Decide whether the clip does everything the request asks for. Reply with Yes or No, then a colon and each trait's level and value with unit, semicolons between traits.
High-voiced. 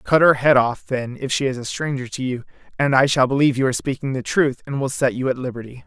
No: low, 130 Hz